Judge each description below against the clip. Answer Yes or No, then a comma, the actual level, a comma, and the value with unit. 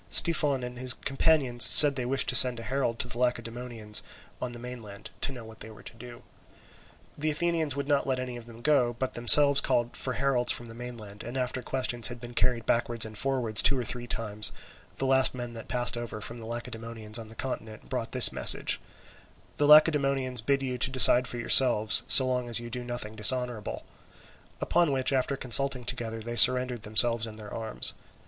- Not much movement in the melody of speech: Yes, narrow, 2.3 semitones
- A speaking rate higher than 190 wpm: Yes, average, 200 wpm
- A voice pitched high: No, low, 120 Hz